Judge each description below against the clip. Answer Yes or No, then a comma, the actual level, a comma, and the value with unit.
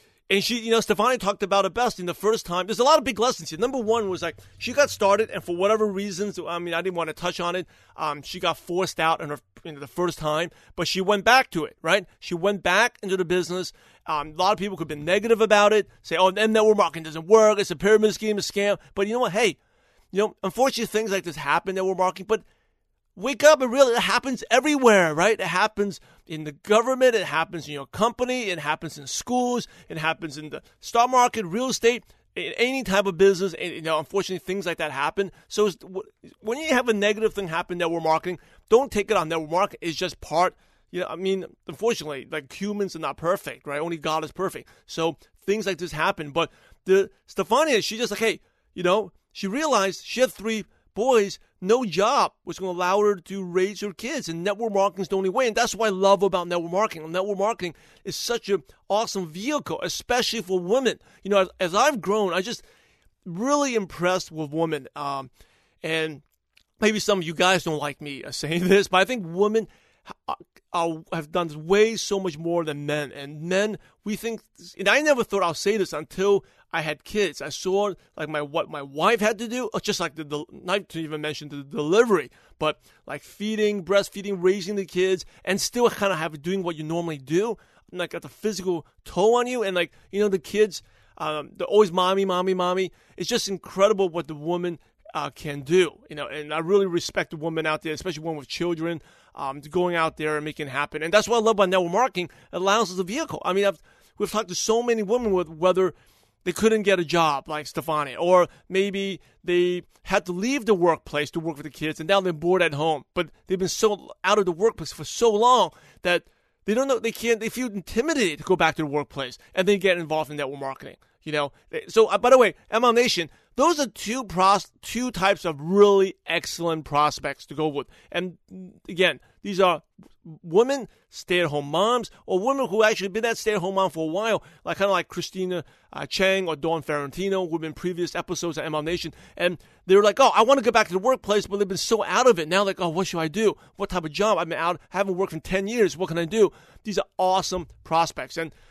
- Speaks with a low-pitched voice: No, medium, 185 Hz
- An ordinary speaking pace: No, fast, 230 wpm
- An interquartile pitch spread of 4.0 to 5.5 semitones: Yes, average, 4.4 semitones